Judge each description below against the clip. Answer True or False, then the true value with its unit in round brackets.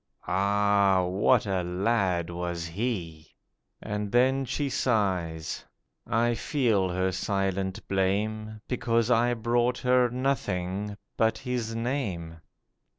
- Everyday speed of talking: False (105 wpm)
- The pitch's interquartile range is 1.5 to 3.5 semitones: False (4.4 semitones)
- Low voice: True (105 Hz)